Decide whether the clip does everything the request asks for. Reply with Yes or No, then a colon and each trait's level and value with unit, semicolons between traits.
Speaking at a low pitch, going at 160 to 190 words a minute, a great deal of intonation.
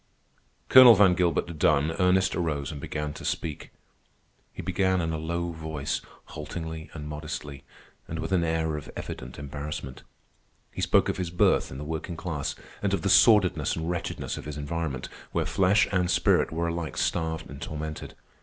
No: very low, 80 Hz; average, 175 wpm; narrow, 2.4 semitones